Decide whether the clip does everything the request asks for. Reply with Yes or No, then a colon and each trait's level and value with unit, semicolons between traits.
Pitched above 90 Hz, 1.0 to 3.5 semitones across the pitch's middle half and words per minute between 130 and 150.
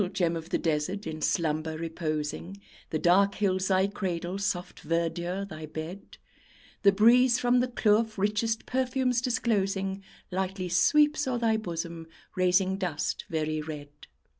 No: high, 190 Hz; average, 4.3 semitones; average, 140 wpm